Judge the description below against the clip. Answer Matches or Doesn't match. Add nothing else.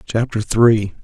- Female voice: Doesn't match